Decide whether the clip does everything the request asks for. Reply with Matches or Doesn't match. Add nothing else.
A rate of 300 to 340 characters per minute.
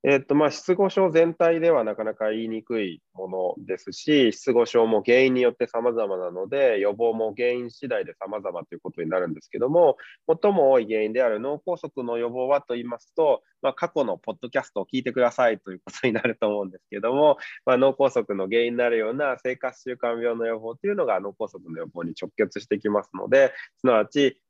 Doesn't match